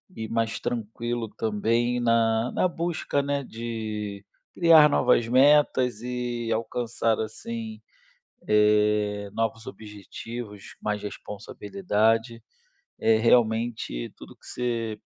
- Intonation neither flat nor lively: No, narrow, 2.1 semitones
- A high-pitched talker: No, low, 115 Hz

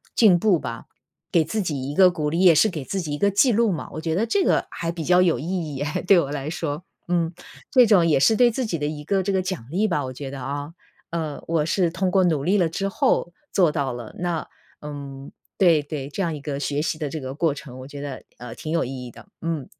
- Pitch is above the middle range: No, medium, 160 Hz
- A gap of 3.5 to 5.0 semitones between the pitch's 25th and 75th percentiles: Yes, average, 4.2 semitones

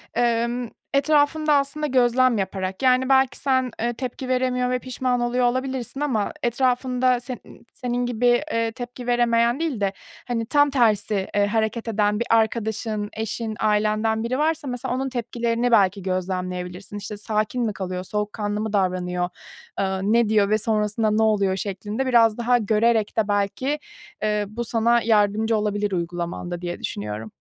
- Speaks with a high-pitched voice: Yes, high, 225 Hz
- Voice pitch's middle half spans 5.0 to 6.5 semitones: No, average, 3.2 semitones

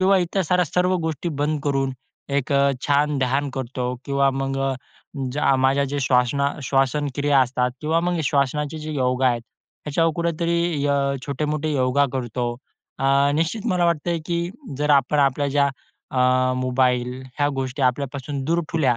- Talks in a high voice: No, medium, 140 Hz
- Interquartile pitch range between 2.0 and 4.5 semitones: Yes, average, 2.8 semitones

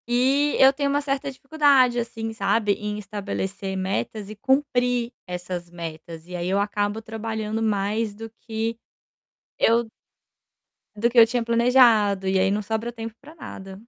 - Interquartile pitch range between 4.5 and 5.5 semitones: No, average, 3.5 semitones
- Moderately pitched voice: No, high, 225 Hz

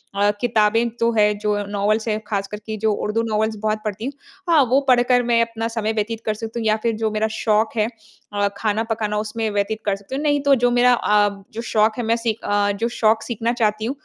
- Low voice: No, high, 220 Hz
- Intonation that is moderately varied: No, narrow, 1.6 semitones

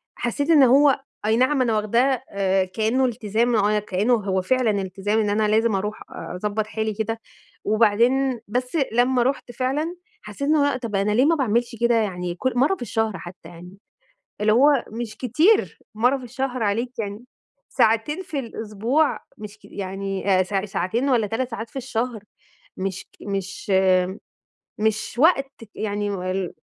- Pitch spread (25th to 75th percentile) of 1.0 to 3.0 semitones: No, average, 3.9 semitones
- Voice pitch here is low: No, high, 225 Hz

